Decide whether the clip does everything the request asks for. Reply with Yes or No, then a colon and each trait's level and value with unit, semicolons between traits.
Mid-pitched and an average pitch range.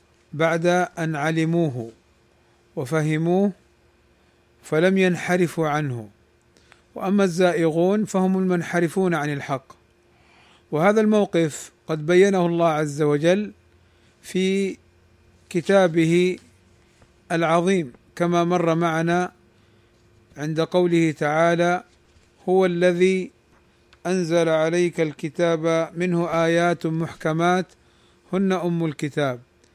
Yes: medium, 165 Hz; average, 3.3 semitones